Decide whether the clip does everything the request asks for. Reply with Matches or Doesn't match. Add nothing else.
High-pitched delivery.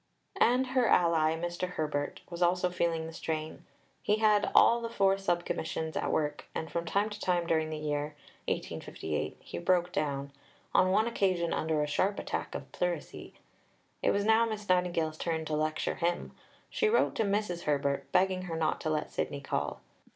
Doesn't match